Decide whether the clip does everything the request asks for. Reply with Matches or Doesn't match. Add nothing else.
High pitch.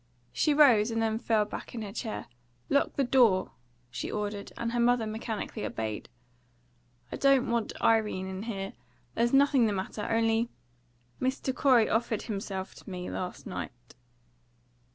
Matches